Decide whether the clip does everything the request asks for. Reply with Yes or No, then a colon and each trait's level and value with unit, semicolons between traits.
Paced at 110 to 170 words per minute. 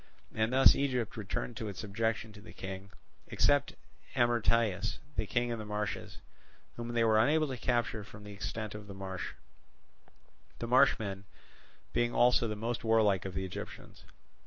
Yes: average, 160 wpm